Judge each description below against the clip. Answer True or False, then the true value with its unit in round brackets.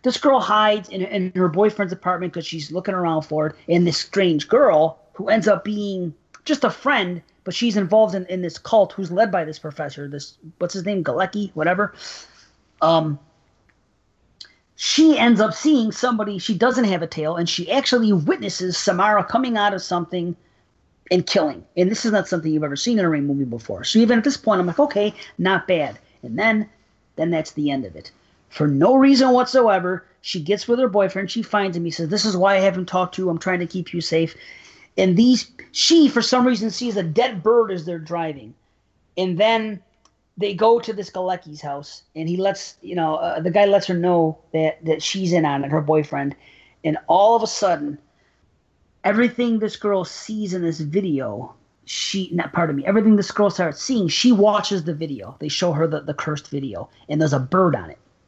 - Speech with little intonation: False (4.7 semitones)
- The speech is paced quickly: True (210 wpm)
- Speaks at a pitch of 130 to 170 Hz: False (185 Hz)